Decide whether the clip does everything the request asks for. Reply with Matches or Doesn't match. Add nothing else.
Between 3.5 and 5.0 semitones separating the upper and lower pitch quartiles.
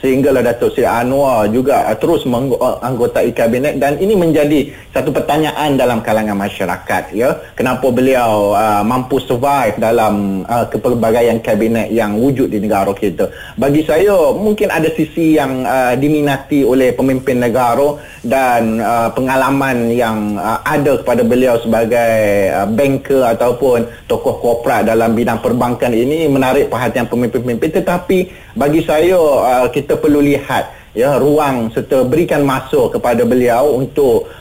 Matches